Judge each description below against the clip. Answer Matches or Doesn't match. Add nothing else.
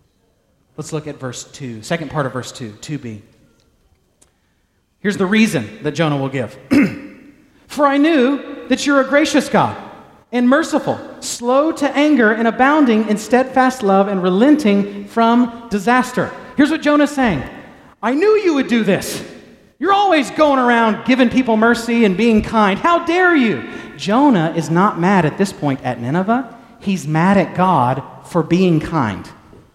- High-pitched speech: Matches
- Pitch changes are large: Matches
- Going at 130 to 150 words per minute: Doesn't match